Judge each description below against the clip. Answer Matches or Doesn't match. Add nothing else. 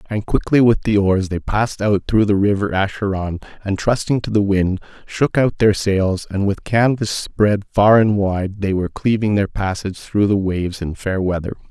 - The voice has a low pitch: Matches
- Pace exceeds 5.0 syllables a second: Doesn't match